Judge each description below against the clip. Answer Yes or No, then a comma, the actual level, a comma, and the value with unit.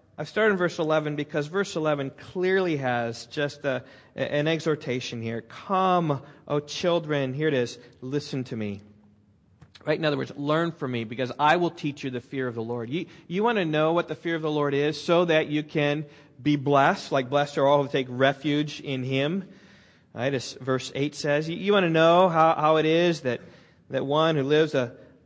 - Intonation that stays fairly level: No, average, 3.4 semitones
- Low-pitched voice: No, medium, 145 Hz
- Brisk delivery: Yes, fast, 210 wpm